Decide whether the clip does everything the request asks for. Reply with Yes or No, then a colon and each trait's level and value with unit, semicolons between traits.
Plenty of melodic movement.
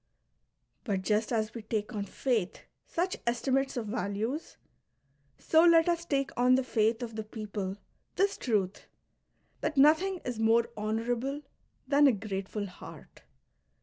No: average, 4.5 semitones